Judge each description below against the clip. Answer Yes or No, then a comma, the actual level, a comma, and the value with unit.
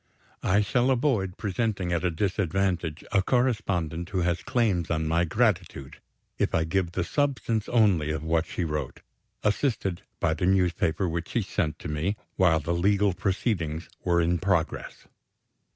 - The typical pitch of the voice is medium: No, very low, 90 Hz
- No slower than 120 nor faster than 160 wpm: Yes, average, 155 wpm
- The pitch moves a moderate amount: Yes, average, 3.9 semitones